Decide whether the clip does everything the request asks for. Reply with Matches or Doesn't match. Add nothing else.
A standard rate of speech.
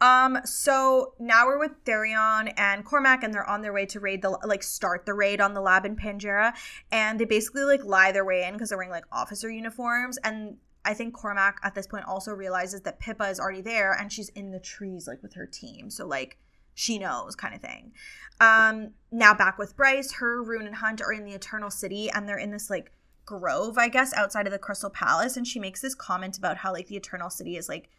Doesn't match